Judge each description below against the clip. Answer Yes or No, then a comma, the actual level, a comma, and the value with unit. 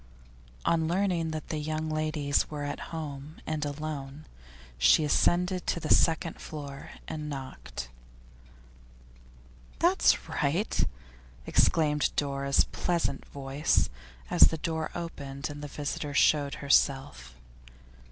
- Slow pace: Yes, slow, 115 wpm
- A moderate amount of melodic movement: No, narrow, 2.3 semitones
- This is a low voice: No, medium, 150 Hz